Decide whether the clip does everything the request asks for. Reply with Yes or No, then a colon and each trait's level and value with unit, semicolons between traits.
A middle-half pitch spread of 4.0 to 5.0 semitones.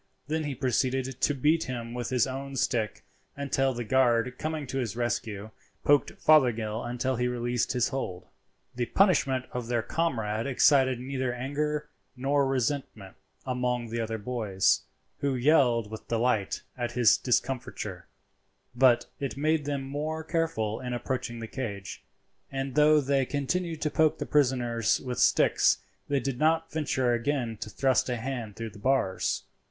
No: average, 3.0 semitones